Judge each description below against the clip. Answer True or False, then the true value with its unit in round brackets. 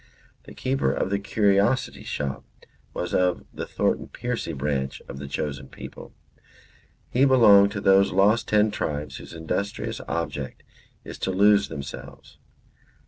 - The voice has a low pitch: True (95 Hz)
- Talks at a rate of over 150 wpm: False (140 wpm)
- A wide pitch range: True (6.0 semitones)